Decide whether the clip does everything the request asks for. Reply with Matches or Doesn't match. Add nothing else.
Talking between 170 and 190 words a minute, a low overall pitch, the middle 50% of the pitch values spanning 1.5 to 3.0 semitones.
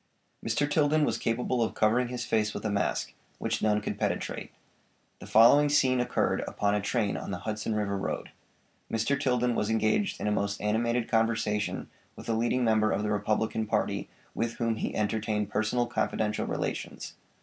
Matches